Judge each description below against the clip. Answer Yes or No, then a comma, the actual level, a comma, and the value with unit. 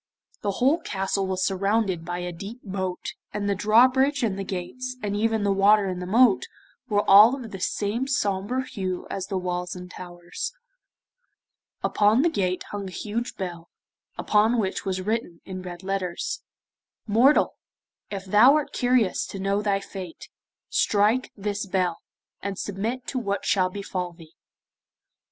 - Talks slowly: No, average, 160 wpm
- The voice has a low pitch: No, high, 200 Hz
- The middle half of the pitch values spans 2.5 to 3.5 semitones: Yes, average, 3.2 semitones